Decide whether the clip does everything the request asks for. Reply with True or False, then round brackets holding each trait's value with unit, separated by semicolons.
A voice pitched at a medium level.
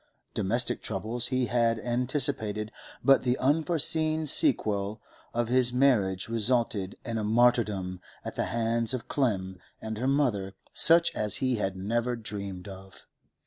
False (115 Hz)